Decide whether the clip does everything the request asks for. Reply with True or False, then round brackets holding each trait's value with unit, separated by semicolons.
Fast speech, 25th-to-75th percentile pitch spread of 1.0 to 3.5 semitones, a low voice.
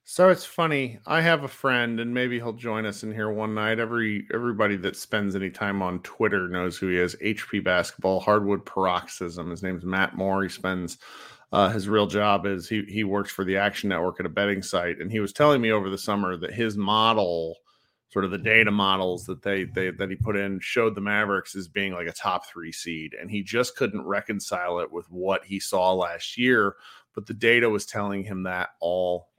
True (220 wpm; 2.7 semitones; 100 Hz)